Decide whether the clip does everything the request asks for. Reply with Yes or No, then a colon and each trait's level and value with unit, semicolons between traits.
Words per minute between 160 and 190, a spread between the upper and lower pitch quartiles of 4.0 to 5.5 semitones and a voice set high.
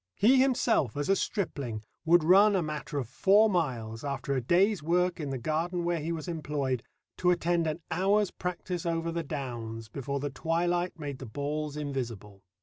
No: average, 180 wpm; average, 4.4 semitones; medium, 155 Hz